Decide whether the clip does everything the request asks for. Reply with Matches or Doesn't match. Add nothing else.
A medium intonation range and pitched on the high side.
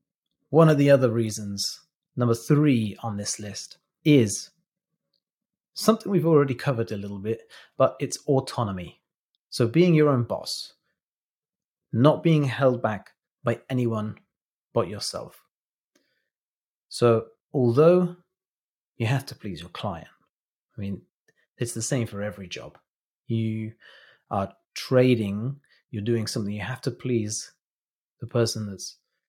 Doesn't match